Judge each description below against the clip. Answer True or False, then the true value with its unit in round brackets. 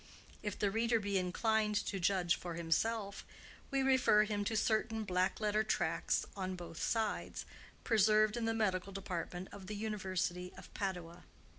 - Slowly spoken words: False (155 wpm)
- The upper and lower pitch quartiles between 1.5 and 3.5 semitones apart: True (2.9 semitones)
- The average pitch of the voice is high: True (205 Hz)